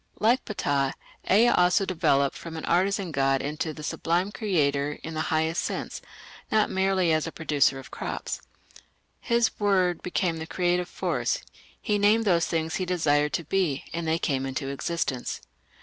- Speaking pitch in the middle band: Yes, medium, 165 Hz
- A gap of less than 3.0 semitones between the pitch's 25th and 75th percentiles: No, average, 4.2 semitones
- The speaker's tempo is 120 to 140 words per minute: No, average, 165 wpm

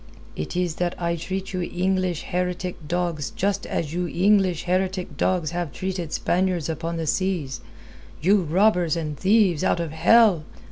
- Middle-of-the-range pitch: Yes, medium, 180 Hz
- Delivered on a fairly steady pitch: Yes, narrow, 2.2 semitones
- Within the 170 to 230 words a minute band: No, average, 155 wpm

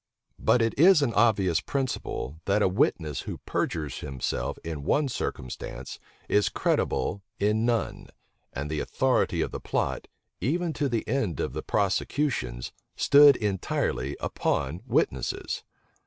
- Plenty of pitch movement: Yes, wide, 9.0 semitones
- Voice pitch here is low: Yes, low, 100 Hz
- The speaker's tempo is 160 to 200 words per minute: No, slow, 135 wpm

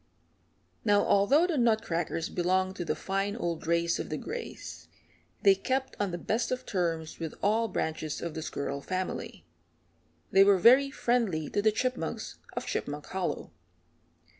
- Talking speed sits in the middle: Yes, average, 155 wpm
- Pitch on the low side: No, high, 195 Hz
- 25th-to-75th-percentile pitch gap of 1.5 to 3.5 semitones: No, average, 5.2 semitones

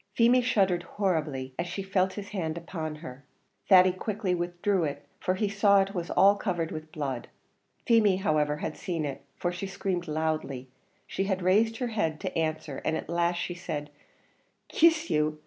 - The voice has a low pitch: No, medium, 175 Hz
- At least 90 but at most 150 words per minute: No, average, 180 wpm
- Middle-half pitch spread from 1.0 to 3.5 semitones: No, average, 4.0 semitones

